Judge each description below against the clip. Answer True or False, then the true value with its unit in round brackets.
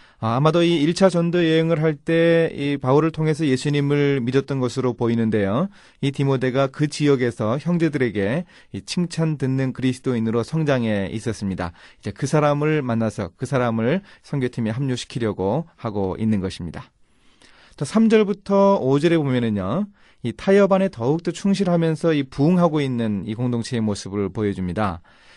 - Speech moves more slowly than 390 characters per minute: True (335 characters per minute)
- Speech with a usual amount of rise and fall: False (6.1 semitones)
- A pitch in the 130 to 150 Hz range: True (135 Hz)